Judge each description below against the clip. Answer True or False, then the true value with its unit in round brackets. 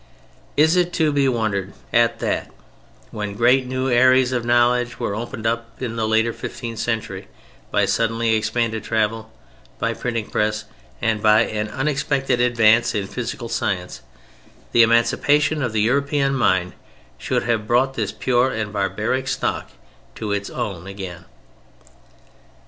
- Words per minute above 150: False (145 wpm)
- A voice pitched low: True (115 Hz)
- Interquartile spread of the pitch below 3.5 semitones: True (2.9 semitones)